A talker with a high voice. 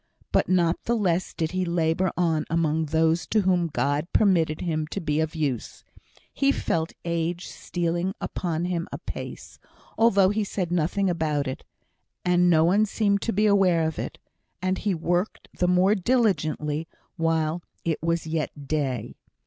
No: medium, 170 Hz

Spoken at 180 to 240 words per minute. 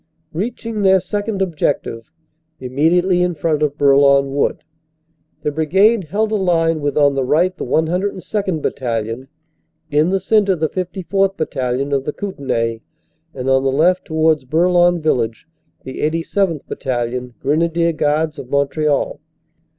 No: average, 145 wpm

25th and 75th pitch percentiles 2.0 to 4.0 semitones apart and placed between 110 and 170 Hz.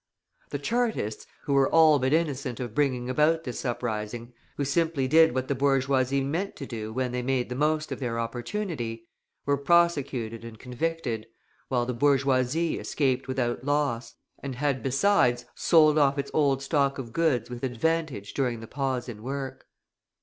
Yes: average, 3.3 semitones; low, 135 Hz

